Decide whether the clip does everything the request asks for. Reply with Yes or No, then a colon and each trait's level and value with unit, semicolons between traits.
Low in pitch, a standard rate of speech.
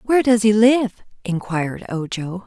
No: high, 210 Hz; average, 145 wpm